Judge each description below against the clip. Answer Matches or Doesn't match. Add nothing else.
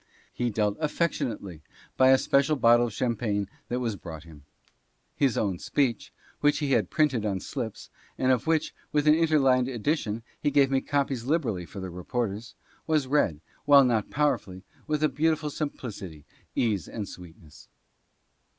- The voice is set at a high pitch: Doesn't match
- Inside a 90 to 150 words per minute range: Doesn't match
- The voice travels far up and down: Matches